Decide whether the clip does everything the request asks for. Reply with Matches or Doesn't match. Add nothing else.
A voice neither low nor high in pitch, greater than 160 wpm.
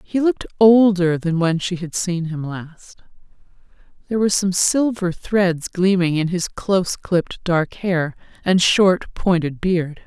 Doesn't match